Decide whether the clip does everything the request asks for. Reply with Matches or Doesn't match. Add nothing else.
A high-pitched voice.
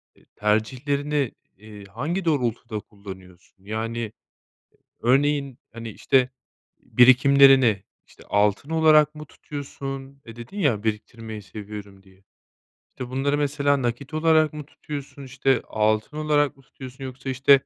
Doesn't match